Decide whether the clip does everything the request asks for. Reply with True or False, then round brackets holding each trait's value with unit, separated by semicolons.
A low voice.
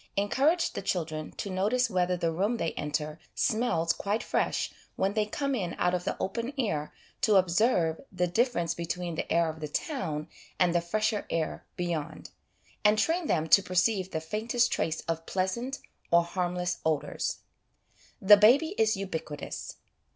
False (185 Hz)